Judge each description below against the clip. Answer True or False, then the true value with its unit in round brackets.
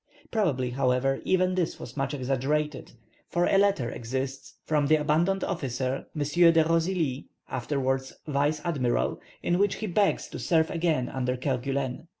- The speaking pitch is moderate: True (145 Hz)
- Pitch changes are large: False (4.4 semitones)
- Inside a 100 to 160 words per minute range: True (150 wpm)